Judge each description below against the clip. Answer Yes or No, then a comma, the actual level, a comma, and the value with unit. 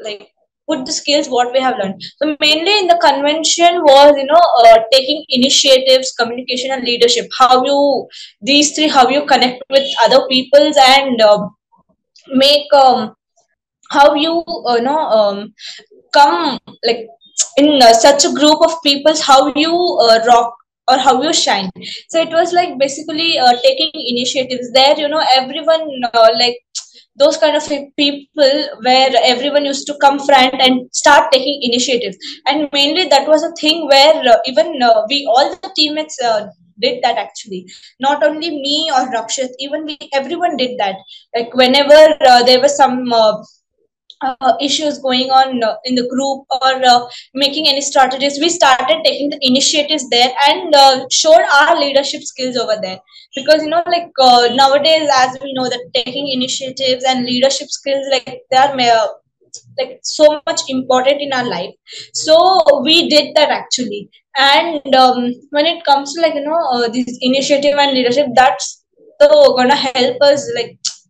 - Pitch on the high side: Yes, very high, 275 Hz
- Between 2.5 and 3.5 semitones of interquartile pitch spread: Yes, average, 3.1 semitones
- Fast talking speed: Yes, fast, 170 wpm